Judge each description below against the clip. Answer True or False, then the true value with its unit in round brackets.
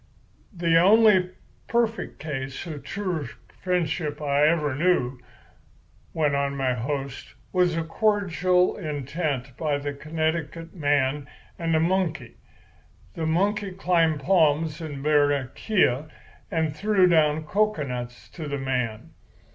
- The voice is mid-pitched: True (155 Hz)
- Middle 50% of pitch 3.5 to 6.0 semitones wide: True (4.0 semitones)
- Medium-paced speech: False (115 wpm)